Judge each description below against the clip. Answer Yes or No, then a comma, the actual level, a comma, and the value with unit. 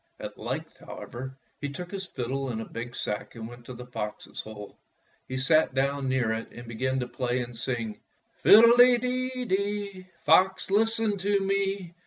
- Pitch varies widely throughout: Yes, wide, 8.6 semitones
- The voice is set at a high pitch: No, low, 135 Hz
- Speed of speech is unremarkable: Yes, average, 180 wpm